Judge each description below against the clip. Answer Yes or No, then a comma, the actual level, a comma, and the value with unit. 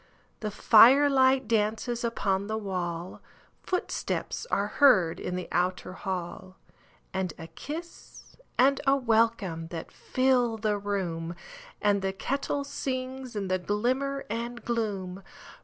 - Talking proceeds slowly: Yes, slow, 110 wpm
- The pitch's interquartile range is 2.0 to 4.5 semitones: No, wide, 5.6 semitones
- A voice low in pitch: No, high, 220 Hz